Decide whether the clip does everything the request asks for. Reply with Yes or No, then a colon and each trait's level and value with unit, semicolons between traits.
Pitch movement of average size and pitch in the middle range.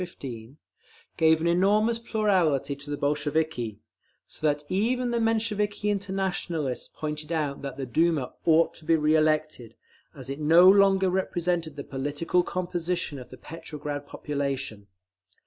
Yes: average, 4.5 semitones; medium, 160 Hz